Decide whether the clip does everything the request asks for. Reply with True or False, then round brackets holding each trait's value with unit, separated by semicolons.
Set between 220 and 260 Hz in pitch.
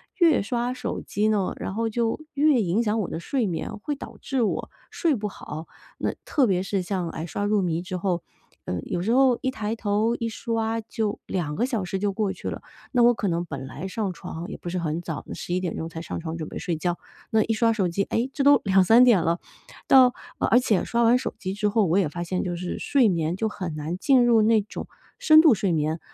False (205 Hz)